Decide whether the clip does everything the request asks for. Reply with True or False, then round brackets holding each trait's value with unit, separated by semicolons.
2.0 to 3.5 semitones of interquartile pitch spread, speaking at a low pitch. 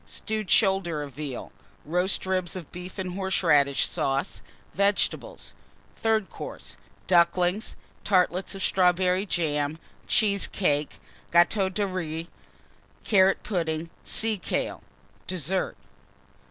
False (2.8 semitones; 180 Hz)